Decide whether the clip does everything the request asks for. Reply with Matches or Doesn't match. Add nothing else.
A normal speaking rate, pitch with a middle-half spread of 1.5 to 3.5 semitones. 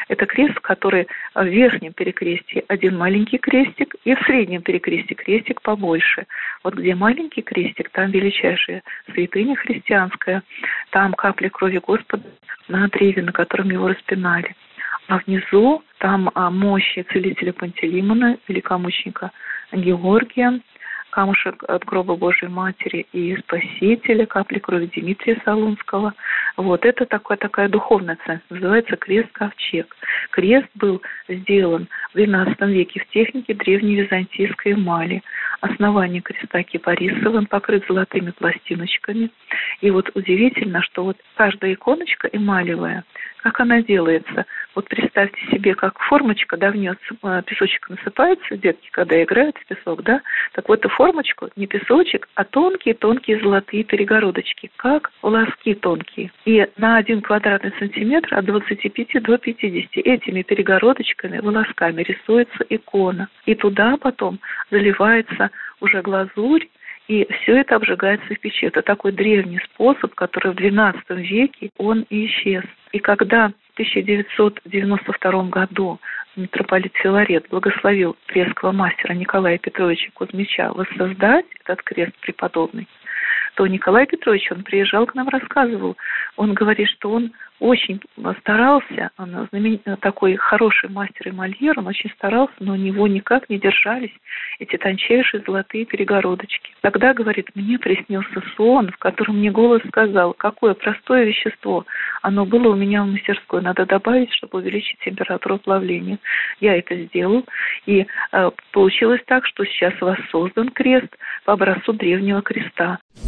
Matches